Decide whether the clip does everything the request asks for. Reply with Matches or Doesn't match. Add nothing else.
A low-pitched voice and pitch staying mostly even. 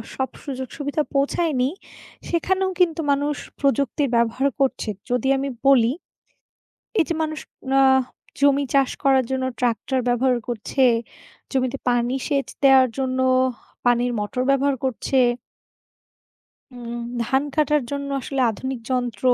Doesn't match